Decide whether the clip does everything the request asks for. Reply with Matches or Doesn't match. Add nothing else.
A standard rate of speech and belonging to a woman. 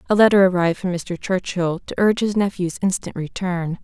Matches